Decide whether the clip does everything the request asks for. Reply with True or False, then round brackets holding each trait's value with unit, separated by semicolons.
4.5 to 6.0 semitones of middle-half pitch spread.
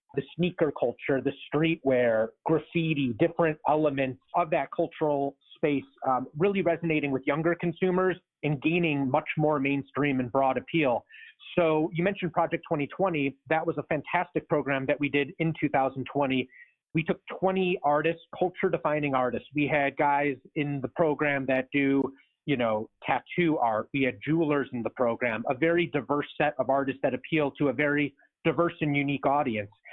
False (3.3 semitones)